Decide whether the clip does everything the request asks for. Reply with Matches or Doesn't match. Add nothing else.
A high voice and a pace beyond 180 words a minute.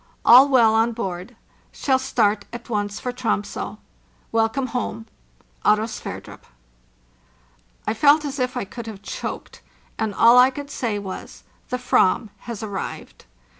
Doesn't match